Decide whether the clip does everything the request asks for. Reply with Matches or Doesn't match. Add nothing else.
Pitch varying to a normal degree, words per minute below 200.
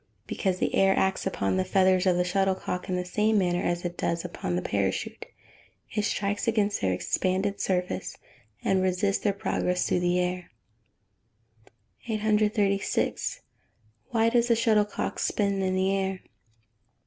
Doesn't match